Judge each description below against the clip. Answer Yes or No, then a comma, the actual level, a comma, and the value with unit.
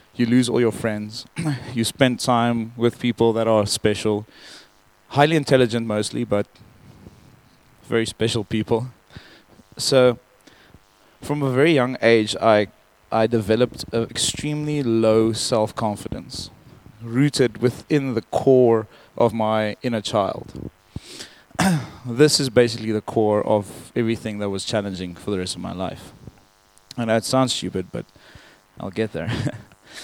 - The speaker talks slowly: Yes, slow, 130 wpm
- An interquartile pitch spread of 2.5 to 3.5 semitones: Yes, average, 2.9 semitones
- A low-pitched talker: Yes, low, 115 Hz